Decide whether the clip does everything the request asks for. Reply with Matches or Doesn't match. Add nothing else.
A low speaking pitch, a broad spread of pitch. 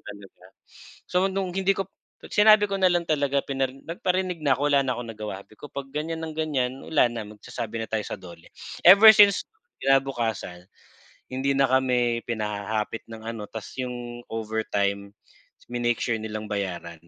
Matches